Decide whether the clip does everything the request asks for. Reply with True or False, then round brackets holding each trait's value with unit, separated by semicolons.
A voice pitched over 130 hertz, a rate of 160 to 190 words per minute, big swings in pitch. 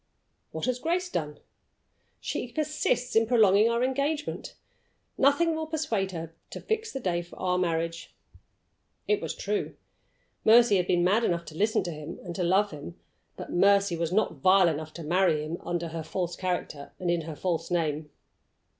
True (185 Hz; 175 wpm; 6.3 semitones)